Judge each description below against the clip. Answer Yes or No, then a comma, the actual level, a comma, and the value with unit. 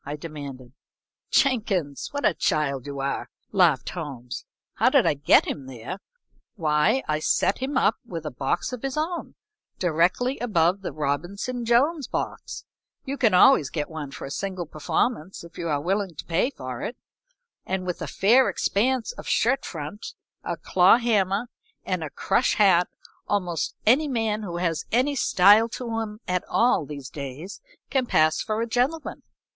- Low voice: No, medium, 185 Hz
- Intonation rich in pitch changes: Yes, wide, 7.6 semitones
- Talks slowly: No, average, 170 wpm